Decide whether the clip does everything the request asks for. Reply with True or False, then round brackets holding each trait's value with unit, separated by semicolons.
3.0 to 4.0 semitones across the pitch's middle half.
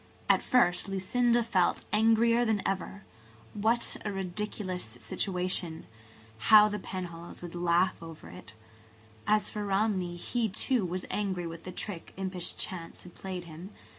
True (3.3 semitones)